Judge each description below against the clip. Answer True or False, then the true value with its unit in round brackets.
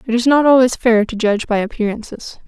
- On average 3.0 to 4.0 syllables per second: False (6.1 syllables/s)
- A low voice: False (230 Hz)